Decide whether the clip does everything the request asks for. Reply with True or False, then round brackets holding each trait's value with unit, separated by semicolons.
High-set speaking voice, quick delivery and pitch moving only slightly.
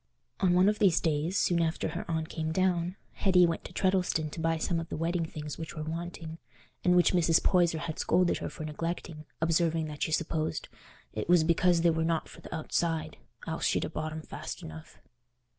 False (165 Hz; 210 wpm; 1.8 semitones)